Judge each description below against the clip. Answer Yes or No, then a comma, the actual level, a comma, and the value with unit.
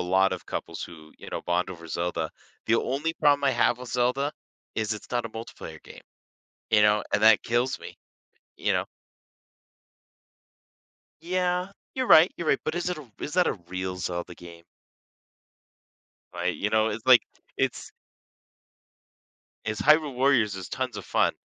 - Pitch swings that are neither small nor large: No, wide, 7.2 semitones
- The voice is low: Yes, low, 115 Hz